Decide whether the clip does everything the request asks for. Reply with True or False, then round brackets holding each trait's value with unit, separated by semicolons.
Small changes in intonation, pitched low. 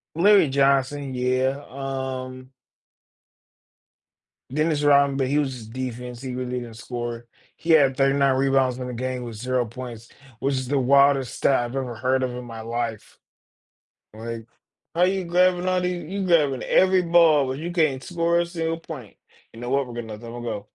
False (3.6 semitones; 130 Hz)